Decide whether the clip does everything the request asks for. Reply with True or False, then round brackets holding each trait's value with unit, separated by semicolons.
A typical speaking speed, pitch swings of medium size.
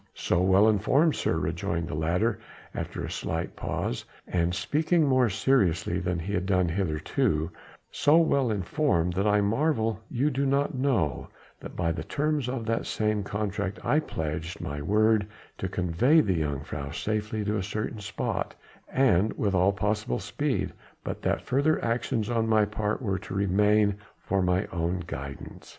True (165 wpm; 4.4 semitones)